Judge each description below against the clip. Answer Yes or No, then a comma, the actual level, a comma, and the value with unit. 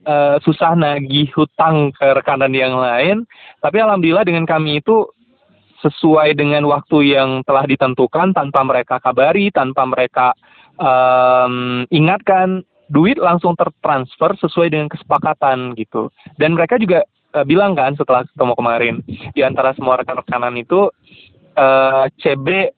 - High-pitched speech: No, medium, 145 Hz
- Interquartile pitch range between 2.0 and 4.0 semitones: No, average, 4.4 semitones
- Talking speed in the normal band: Yes, average, 130 wpm